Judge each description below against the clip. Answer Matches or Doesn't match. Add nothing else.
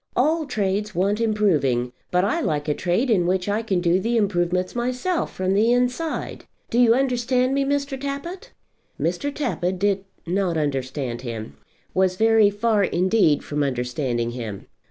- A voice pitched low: Doesn't match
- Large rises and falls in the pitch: Matches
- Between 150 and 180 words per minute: Matches